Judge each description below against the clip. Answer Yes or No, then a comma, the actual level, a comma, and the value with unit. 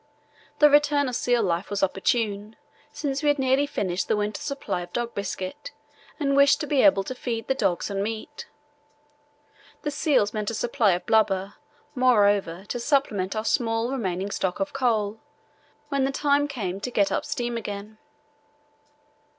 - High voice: Yes, high, 225 Hz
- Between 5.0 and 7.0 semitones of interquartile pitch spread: Yes, average, 5.3 semitones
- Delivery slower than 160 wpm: No, average, 165 wpm